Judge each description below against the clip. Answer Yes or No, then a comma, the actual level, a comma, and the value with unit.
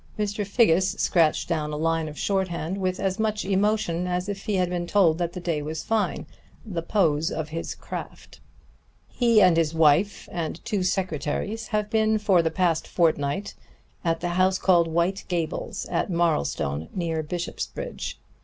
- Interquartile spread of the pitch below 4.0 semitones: Yes, average, 3.4 semitones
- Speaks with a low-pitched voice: No, medium, 180 Hz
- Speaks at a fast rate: No, average, 165 wpm